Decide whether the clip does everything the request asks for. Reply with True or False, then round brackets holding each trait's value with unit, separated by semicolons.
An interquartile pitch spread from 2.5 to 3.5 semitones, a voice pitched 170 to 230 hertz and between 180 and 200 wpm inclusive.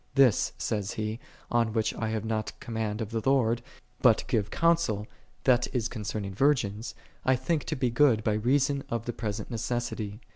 False (3.1 semitones; 115 Hz; 185 wpm)